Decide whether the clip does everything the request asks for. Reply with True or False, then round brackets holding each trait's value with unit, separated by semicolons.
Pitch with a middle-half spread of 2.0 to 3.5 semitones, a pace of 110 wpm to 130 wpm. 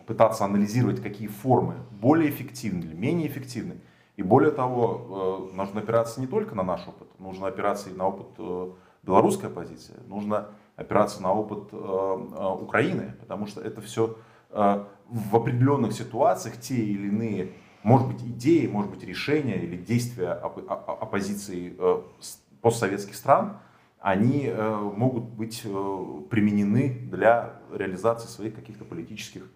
True (2.7 semitones; 125 wpm)